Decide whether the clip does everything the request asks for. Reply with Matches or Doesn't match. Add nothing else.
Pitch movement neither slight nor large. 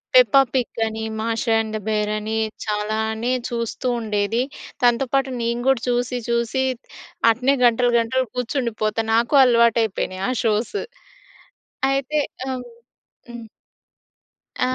Doesn't match